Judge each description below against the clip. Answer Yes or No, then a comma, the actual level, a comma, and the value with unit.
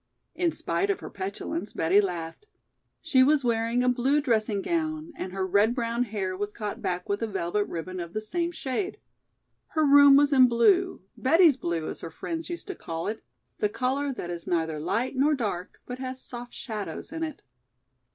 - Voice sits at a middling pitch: No, high, 235 Hz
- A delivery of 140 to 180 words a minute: No, average, 190 wpm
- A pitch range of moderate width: No, wide, 6.8 semitones